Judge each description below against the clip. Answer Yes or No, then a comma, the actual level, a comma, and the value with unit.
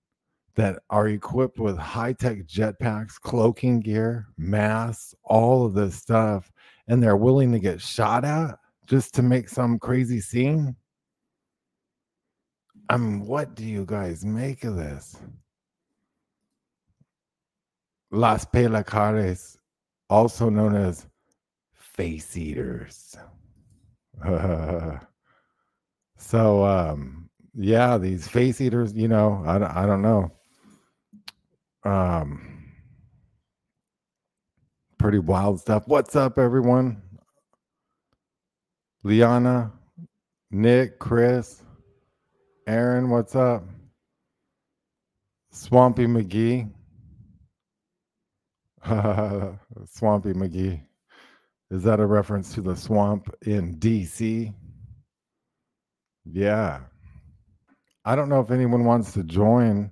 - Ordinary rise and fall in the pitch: Yes, average, 3.6 semitones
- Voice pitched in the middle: No, low, 110 Hz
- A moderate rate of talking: No, slow, 90 wpm